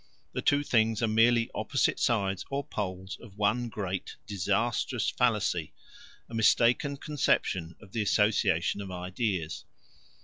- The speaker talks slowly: Yes, slow, 130 wpm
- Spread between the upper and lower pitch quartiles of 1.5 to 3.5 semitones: No, average, 3.9 semitones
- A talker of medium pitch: No, low, 105 Hz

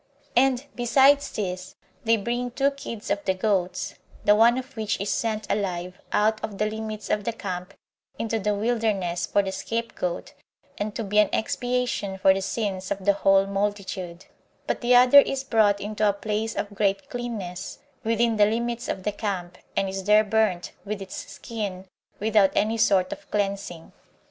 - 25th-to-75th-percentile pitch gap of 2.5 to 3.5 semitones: Yes, average, 2.8 semitones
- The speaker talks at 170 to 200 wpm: Yes, average, 175 wpm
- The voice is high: Yes, high, 210 Hz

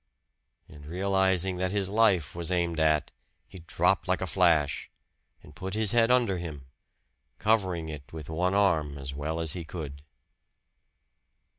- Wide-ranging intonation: No, average, 3.7 semitones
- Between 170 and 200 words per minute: No, average, 150 wpm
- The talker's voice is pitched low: Yes, very low, 85 Hz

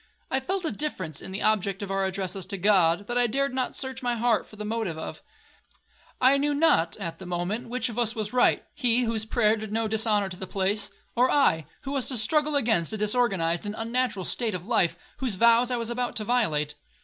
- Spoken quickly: Yes, fast, 220 wpm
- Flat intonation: No, average, 4.2 semitones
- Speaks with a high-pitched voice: Yes, high, 220 Hz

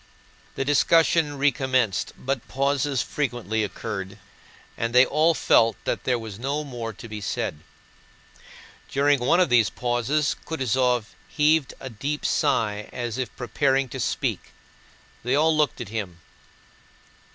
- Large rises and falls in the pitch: No, average, 4.1 semitones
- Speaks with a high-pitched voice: No, low, 130 Hz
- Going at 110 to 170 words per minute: Yes, slow, 135 wpm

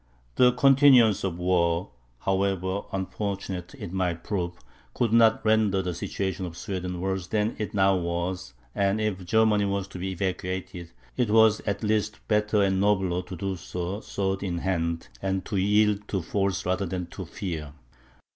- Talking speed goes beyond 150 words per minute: Yes, average, 165 wpm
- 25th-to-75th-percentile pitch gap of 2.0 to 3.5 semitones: Yes, narrow, 2.5 semitones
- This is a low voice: Yes, very low, 95 Hz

